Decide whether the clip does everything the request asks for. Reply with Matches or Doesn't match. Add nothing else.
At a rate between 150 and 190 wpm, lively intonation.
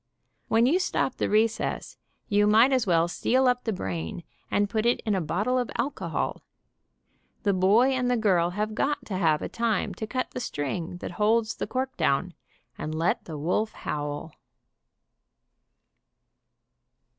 Matches